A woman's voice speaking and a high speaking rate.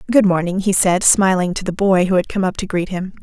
Yes: female; fast, 280 wpm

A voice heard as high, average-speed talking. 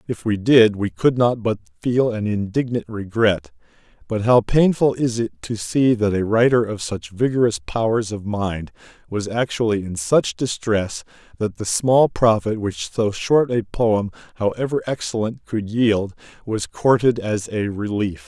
No: low, 110 Hz; average, 165 wpm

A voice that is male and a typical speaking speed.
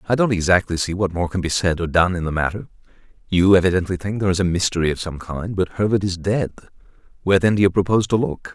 No: male; fast, 245 wpm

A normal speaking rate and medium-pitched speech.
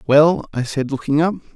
Yes: average, 195 wpm; medium, 150 Hz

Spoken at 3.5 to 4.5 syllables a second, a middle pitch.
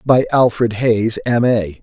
No: 3.7 syllables/s; low, 115 Hz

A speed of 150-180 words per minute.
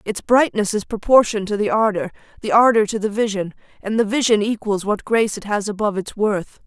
No: fast, 205 wpm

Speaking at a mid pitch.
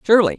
Yes: medium, 175 Hz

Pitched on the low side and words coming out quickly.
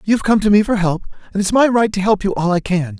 No: high, 200 Hz; fast, 320 wpm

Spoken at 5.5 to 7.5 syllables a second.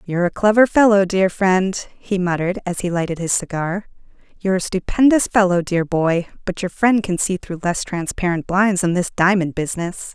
No: 5.2 syllables/s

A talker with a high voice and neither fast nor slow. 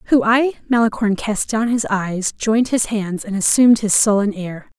Yes: high, 215 Hz; average, 190 wpm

